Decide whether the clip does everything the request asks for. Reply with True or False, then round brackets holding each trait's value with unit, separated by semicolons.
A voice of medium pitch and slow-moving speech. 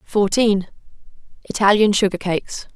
False (200 Hz; 65 wpm)